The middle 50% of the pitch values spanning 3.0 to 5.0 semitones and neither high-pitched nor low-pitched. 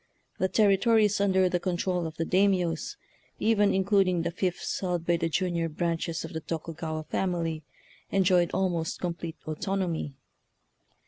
No: narrow, 2.5 semitones; medium, 175 Hz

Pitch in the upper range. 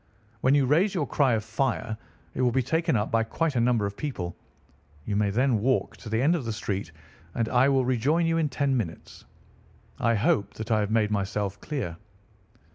No: low, 120 Hz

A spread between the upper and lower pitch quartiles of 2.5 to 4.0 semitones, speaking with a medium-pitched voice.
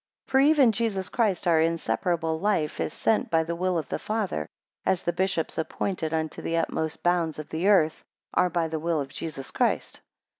Yes: average, 3.2 semitones; medium, 170 Hz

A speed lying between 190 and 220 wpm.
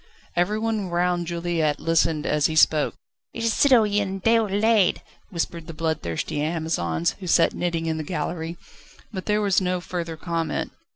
No: average, 150 wpm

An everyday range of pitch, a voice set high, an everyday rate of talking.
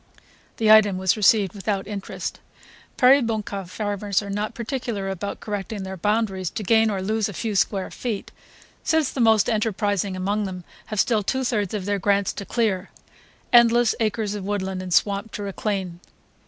No: narrow, 2.2 semitones; high, 205 Hz; average, 170 wpm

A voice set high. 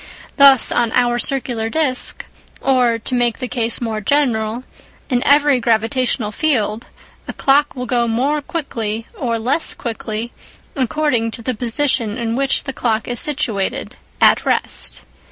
Yes: high, 245 Hz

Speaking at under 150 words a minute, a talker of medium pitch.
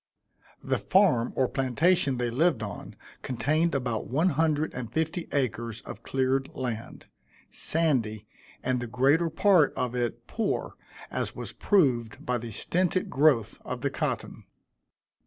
No: average, 140 wpm; low, 130 Hz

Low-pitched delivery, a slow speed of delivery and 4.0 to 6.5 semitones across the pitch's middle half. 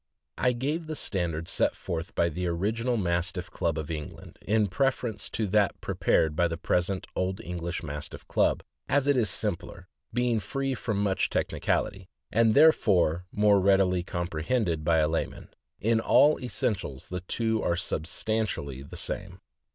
No: very low, 95 Hz; average, 160 wpm; average, 4.8 semitones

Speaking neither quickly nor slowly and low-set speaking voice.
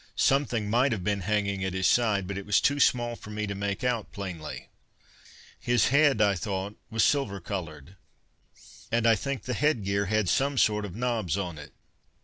Yes: average, 185 wpm; low, 105 Hz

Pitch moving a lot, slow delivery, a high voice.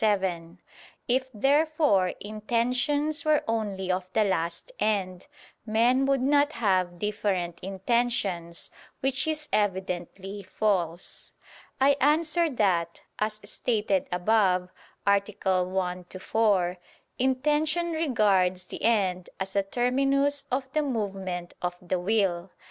Yes: wide, 6.1 semitones; slow, 115 wpm; high, 210 Hz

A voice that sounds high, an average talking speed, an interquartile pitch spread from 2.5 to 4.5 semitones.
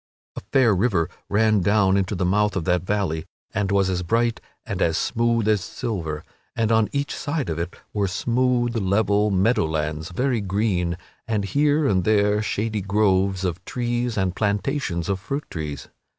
No: low, 100 Hz; average, 175 wpm; average, 3.8 semitones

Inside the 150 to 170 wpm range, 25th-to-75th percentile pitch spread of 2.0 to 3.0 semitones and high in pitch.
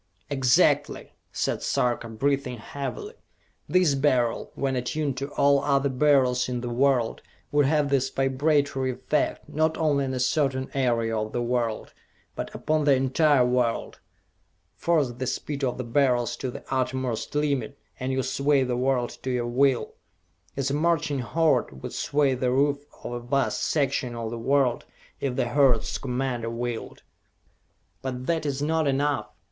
No: average, 160 wpm; narrow, 2.5 semitones; low, 135 Hz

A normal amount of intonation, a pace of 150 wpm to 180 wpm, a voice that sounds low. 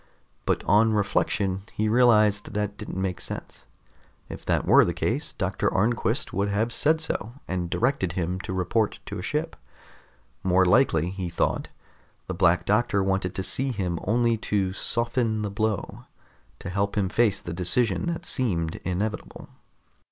Yes: average, 3.3 semitones; average, 160 wpm; low, 100 Hz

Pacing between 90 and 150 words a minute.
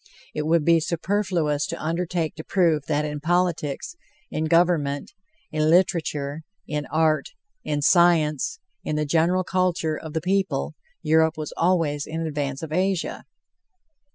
Yes: average, 140 wpm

